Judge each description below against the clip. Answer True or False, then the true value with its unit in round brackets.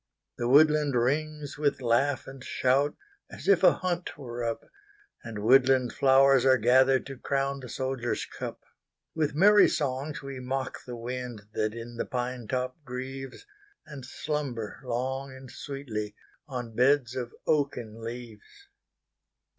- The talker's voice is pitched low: True (130 Hz)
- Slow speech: True (120 wpm)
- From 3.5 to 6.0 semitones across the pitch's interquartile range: False (2.9 semitones)